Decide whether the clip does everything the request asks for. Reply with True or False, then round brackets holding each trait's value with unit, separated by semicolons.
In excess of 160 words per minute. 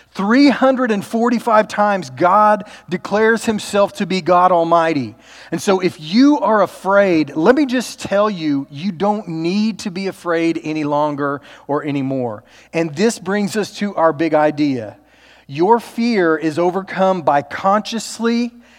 False (140 wpm)